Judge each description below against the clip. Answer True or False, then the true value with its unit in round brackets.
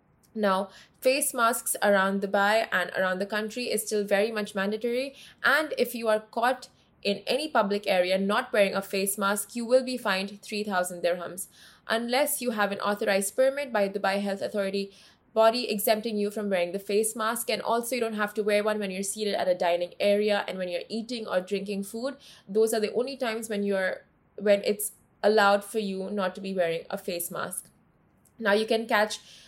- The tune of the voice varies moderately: False (2.3 semitones)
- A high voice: True (205 Hz)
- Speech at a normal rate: False (200 wpm)